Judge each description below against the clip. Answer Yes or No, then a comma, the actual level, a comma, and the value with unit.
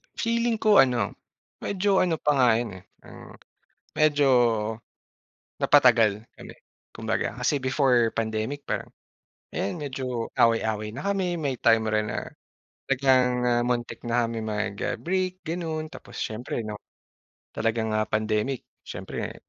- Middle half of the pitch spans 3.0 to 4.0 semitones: No, wide, 5.6 semitones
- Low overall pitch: Yes, low, 125 Hz